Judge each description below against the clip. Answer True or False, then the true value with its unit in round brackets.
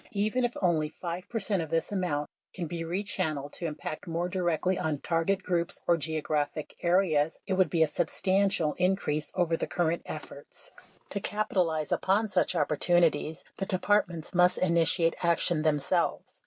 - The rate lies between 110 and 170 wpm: True (165 wpm)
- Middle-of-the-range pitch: True (170 Hz)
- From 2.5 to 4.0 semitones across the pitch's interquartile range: True (2.9 semitones)